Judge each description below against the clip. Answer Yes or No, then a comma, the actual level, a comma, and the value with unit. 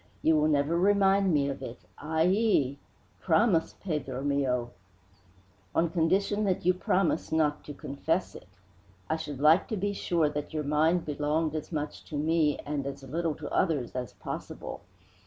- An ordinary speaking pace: Yes, average, 165 wpm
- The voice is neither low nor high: Yes, medium, 155 Hz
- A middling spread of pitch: Yes, average, 3.2 semitones